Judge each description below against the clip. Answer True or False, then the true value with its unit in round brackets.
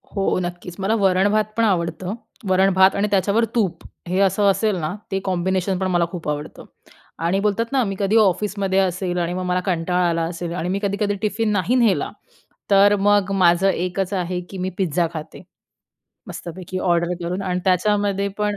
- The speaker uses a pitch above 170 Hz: True (190 Hz)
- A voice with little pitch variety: True (2.2 semitones)